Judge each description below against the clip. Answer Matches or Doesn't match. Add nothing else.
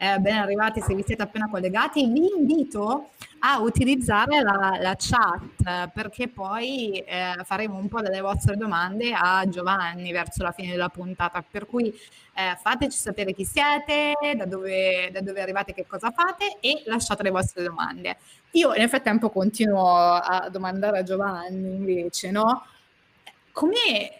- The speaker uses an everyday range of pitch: Matches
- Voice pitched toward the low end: Doesn't match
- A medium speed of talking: Matches